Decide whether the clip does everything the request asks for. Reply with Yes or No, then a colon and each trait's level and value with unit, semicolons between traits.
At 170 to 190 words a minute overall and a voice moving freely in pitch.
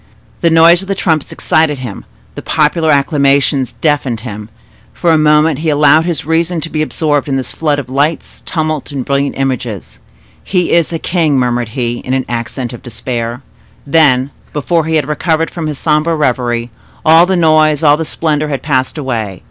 No: average, 180 wpm; average, 3.8 semitones